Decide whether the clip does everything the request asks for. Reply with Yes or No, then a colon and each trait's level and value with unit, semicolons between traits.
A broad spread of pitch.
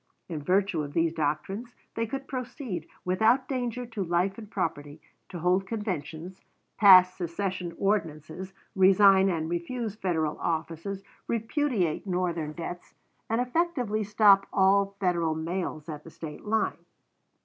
No: average, 4.5 semitones